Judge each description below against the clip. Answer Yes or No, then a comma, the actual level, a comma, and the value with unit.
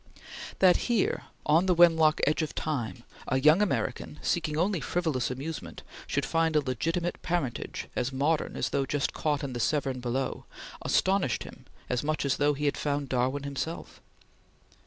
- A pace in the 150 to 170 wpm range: Yes, average, 165 wpm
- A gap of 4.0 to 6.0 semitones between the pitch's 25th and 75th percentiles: No, average, 3.6 semitones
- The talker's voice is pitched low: No, medium, 150 Hz